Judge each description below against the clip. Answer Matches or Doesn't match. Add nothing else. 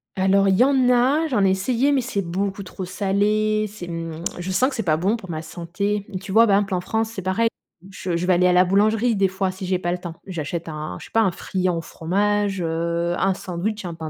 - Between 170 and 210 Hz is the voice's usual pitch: Matches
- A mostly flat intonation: Doesn't match